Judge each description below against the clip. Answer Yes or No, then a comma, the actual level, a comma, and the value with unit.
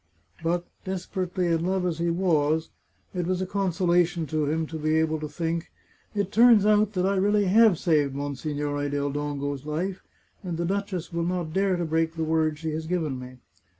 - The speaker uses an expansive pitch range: No, average, 3.2 semitones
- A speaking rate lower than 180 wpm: No, average, 195 wpm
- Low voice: No, medium, 170 Hz